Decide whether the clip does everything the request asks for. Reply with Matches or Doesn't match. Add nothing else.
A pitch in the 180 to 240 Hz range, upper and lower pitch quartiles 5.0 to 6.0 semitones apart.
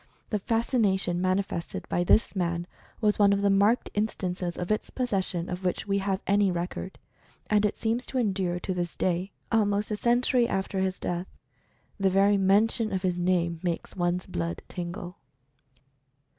Doesn't match